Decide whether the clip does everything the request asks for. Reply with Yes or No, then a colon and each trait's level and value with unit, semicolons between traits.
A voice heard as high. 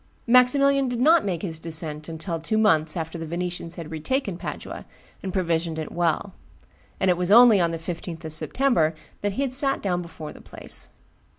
No: medium, 175 Hz